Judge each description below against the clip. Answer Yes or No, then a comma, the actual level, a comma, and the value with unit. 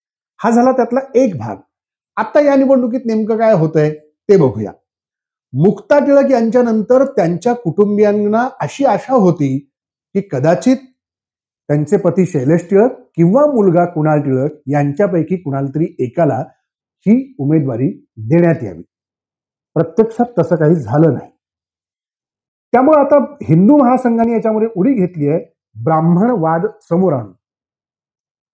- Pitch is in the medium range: Yes, medium, 180 Hz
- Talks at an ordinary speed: No, slow, 120 wpm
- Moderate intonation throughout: No, wide, 7.8 semitones